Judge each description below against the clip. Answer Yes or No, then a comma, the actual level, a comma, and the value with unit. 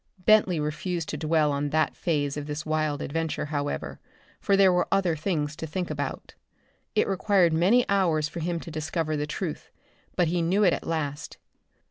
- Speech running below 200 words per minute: Yes, average, 180 wpm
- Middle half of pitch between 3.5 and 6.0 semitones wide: No, average, 3.0 semitones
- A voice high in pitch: No, medium, 160 Hz